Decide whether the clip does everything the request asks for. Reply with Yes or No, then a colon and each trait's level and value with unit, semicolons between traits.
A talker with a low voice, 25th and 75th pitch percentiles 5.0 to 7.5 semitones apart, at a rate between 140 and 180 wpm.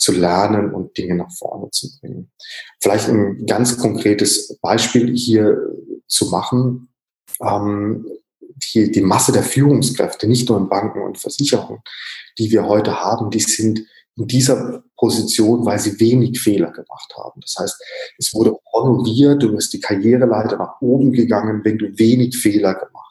No: low, 110 Hz; average, 2.8 semitones; average, 155 wpm